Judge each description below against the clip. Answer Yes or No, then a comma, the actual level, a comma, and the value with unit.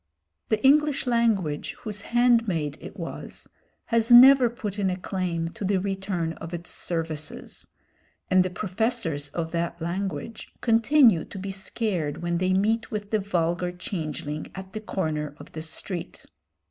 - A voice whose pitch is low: No, high, 190 Hz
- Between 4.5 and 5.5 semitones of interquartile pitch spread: Yes, average, 4.8 semitones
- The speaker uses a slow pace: No, average, 150 wpm